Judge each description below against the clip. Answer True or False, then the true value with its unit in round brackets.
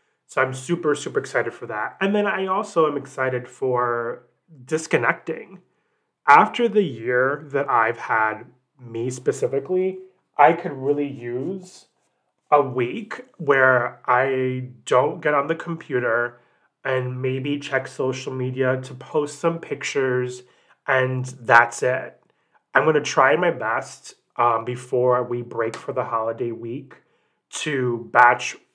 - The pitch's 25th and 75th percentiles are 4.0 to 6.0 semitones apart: False (3.1 semitones)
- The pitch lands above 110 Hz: True (130 Hz)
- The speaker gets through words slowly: True (130 wpm)